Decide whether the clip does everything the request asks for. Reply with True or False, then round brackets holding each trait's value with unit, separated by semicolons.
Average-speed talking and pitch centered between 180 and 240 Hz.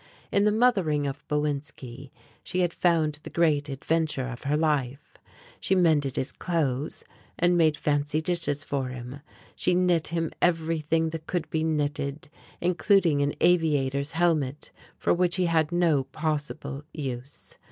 False (145 wpm; 155 Hz)